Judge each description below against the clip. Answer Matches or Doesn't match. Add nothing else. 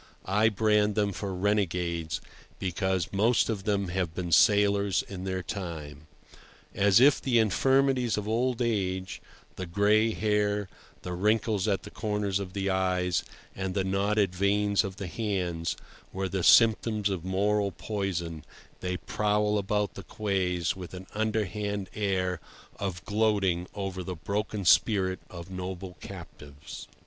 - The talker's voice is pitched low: Matches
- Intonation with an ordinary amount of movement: Doesn't match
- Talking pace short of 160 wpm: Matches